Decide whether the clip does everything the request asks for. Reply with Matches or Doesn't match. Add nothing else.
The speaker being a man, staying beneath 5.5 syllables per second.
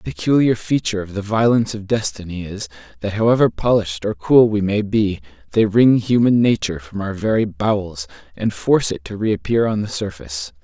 Doesn't match